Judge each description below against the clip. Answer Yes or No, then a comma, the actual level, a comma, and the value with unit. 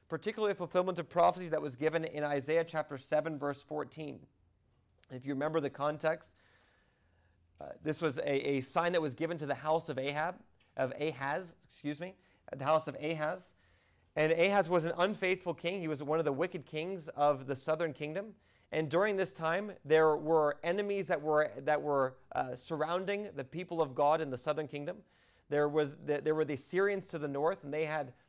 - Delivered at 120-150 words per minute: No, average, 195 wpm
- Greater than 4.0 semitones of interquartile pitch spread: No, average, 3.0 semitones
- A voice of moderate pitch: Yes, medium, 155 Hz